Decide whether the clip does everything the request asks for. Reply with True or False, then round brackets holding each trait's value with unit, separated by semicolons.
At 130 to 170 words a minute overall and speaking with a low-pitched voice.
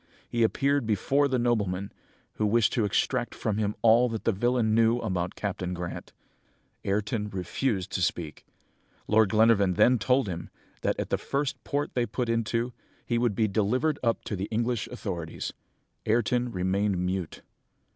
True (160 wpm; 110 Hz)